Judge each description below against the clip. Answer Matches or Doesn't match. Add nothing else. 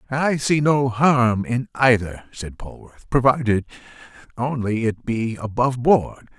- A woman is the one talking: Doesn't match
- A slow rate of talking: Matches